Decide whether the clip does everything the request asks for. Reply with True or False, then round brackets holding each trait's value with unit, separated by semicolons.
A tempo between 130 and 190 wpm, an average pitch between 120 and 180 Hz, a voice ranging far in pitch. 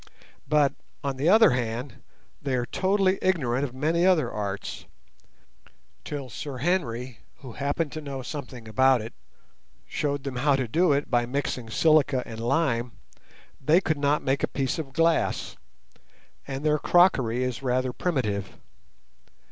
False (150 wpm; 135 Hz; 3.9 semitones)